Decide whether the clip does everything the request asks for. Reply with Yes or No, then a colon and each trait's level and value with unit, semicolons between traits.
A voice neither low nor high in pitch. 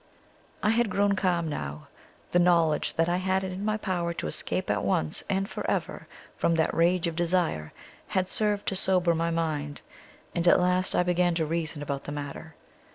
Yes: medium, 175 Hz